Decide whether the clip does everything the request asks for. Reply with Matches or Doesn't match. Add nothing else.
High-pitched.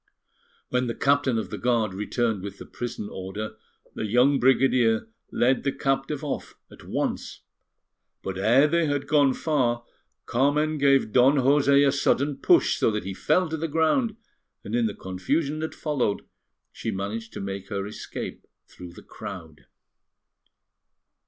Doesn't match